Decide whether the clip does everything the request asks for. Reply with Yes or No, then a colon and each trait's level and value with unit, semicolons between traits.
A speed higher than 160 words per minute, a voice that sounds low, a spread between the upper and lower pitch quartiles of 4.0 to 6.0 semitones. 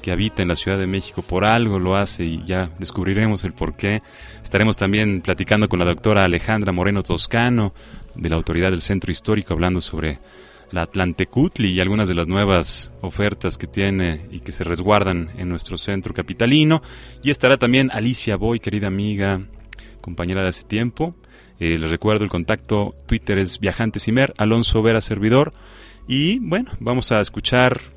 No: average, 170 wpm; low, 100 Hz; average, 3.5 semitones